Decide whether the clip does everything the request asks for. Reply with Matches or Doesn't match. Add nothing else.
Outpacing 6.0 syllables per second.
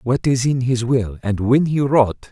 Doesn't match